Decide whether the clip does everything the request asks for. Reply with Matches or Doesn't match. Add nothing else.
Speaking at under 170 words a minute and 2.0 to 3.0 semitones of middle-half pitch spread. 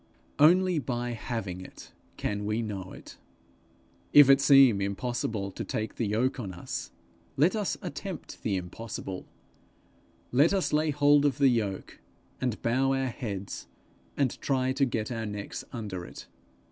Doesn't match